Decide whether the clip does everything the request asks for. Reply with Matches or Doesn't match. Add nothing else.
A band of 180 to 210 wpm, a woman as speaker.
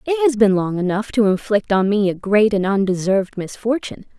Matches